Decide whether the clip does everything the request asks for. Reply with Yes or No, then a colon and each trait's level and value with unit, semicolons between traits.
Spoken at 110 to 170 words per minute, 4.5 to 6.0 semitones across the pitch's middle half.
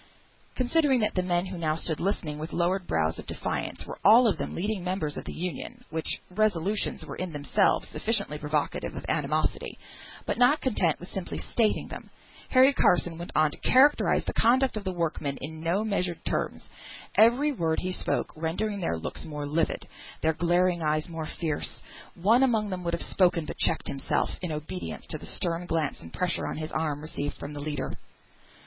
No: average, 190 wpm; average, 5.0 semitones